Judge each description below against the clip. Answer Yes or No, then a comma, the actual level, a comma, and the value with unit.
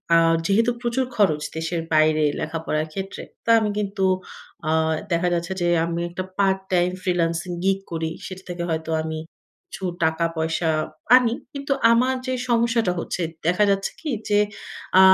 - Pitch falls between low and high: Yes, medium, 180 Hz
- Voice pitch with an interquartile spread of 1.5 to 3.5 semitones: No, average, 4.2 semitones